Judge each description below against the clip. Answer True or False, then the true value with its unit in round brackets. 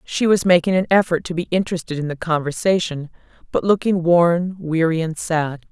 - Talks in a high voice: False (170 Hz)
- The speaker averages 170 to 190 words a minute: True (180 wpm)